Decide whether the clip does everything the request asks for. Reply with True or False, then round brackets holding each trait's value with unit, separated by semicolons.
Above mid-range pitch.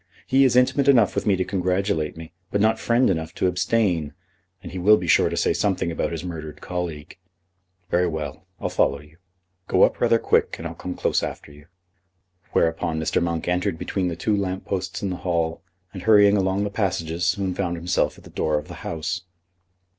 False (90 Hz)